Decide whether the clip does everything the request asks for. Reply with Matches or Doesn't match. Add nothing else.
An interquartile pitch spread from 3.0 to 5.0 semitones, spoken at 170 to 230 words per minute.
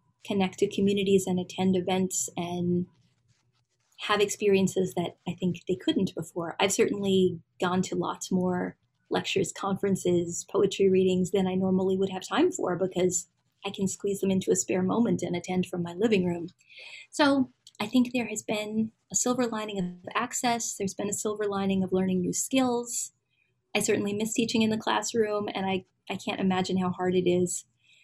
Doesn't match